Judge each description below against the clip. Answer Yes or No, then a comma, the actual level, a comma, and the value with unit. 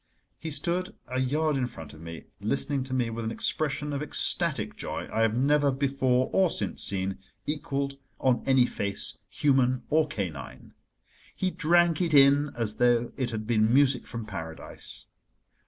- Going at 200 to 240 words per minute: No, average, 165 wpm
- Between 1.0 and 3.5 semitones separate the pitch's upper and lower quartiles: No, average, 4.5 semitones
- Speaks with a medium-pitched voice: No, low, 130 Hz